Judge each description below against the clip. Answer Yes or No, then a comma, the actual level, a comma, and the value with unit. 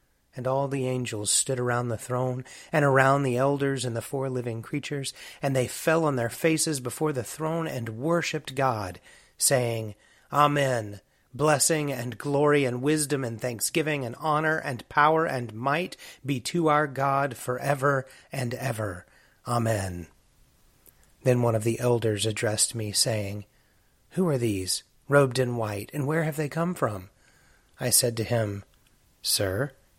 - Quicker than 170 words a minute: No, average, 155 wpm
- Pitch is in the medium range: No, low, 130 Hz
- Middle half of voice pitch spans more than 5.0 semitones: No, average, 4.0 semitones